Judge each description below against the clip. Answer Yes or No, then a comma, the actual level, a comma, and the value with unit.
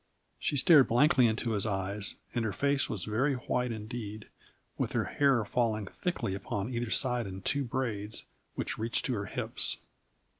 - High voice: No, low, 115 Hz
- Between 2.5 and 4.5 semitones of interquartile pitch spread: Yes, average, 3.6 semitones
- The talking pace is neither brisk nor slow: Yes, average, 165 wpm